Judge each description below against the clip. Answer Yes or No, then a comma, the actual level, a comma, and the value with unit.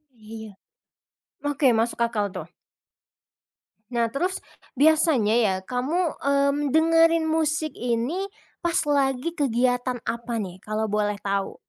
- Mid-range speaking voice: No, very high, 255 Hz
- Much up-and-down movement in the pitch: Yes, wide, 5.8 semitones